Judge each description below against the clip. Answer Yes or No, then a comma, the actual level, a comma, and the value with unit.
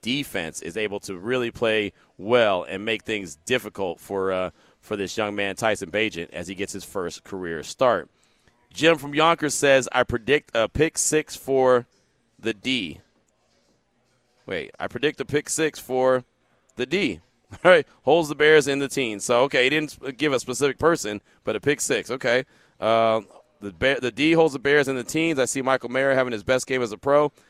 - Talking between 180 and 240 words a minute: Yes, average, 195 wpm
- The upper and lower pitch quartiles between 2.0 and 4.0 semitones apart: No, average, 4.9 semitones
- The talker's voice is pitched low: Yes, low, 125 Hz